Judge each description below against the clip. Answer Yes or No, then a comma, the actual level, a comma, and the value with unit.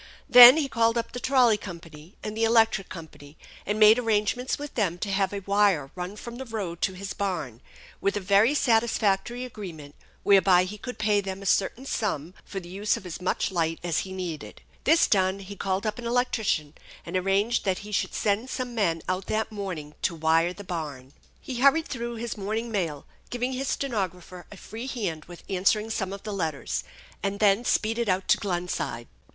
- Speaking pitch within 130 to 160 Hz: No, high, 200 Hz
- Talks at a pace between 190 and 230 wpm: Yes, average, 200 wpm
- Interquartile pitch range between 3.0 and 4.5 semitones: Yes, average, 4.0 semitones